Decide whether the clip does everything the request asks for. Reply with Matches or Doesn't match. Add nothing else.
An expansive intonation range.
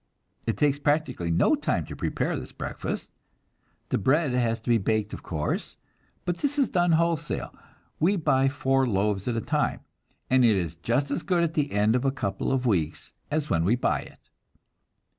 Matches